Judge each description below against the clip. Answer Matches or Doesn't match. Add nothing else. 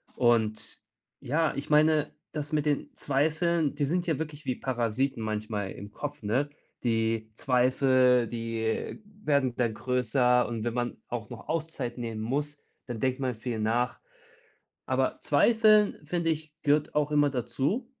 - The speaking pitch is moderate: Doesn't match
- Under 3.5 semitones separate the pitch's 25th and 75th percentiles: Doesn't match